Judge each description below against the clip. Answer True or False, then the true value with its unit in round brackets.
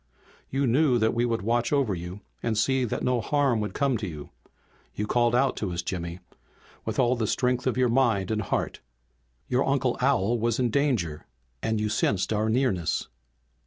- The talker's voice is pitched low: True (120 Hz)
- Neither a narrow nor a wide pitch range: True (3.3 semitones)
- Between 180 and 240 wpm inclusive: True (190 wpm)